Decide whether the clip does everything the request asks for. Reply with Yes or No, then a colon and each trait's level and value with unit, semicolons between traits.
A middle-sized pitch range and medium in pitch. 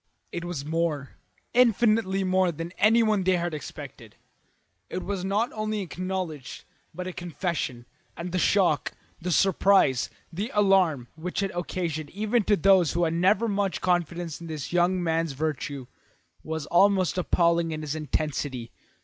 Yes: average, 3.5 semitones; medium, 175 Hz